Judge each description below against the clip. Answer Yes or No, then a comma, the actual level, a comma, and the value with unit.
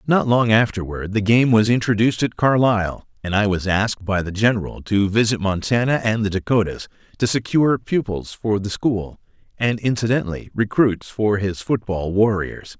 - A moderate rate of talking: Yes, average, 165 wpm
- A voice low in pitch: Yes, low, 110 Hz